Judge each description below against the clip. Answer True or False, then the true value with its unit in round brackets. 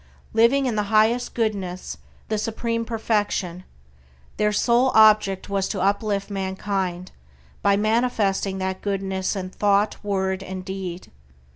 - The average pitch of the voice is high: True (200 Hz)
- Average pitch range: False (2.3 semitones)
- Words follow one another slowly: True (125 wpm)